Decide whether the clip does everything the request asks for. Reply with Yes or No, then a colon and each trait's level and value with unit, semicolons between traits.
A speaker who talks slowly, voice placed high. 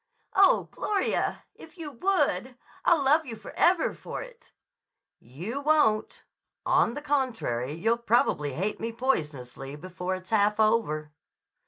Yes: slow, 130 wpm; high, 225 Hz